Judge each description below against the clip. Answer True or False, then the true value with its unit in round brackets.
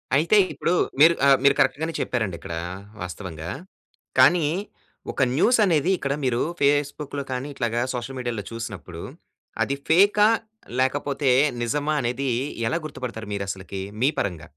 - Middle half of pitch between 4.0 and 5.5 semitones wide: True (4.6 semitones)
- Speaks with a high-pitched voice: False (135 Hz)